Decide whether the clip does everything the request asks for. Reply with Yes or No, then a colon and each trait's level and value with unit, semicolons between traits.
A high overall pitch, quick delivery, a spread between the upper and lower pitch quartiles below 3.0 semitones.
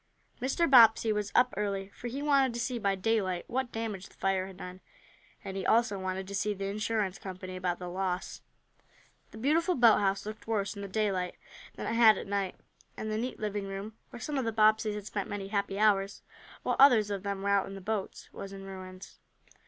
Yes: high, 205 Hz; fast, 215 wpm; narrow, 2.5 semitones